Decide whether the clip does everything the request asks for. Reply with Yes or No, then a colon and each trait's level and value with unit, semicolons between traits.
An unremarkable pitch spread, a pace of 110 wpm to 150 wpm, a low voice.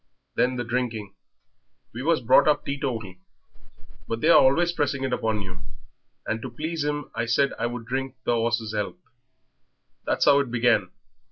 No: average, 3.6 semitones; average, 165 wpm; low, 125 Hz